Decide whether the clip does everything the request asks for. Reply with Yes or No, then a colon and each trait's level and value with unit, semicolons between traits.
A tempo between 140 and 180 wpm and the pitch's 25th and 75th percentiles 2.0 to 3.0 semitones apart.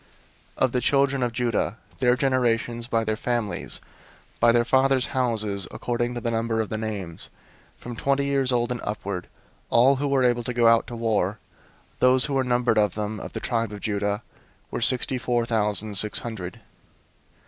No: average, 190 wpm; average, 2.7 semitones